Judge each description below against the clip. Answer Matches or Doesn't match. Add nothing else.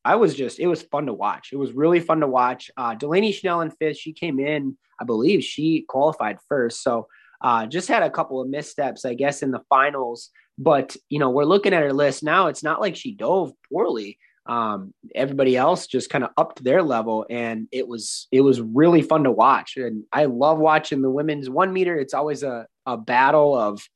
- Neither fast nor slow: Doesn't match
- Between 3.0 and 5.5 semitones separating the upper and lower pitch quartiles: Matches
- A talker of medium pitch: Matches